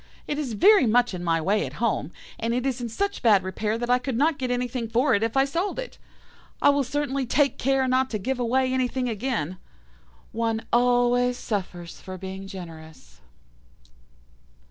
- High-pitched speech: Yes, high, 245 Hz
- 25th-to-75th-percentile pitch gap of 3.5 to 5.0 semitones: Yes, average, 4.1 semitones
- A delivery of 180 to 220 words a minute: Yes, average, 185 wpm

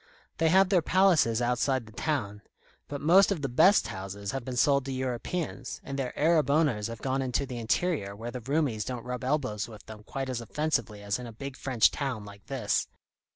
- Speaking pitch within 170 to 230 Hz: No, low, 130 Hz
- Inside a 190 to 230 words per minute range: Yes, fast, 205 wpm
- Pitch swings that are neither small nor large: Yes, average, 4.6 semitones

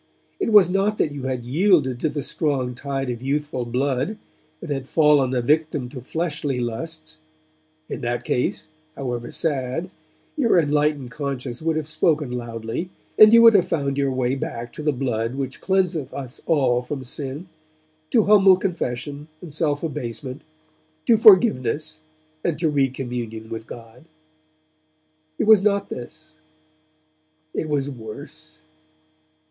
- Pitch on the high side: No, medium, 140 Hz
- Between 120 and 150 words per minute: Yes, average, 145 wpm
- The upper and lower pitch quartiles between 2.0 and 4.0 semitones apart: No, average, 4.4 semitones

